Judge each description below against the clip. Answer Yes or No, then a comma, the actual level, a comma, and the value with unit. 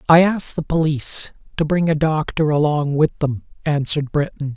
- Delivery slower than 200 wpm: Yes, average, 170 wpm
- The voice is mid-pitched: Yes, medium, 155 Hz